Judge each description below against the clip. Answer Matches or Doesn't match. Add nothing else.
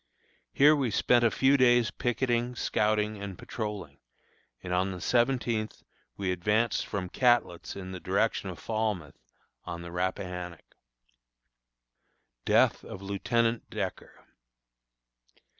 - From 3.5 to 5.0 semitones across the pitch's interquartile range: Matches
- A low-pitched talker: Matches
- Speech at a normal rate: Doesn't match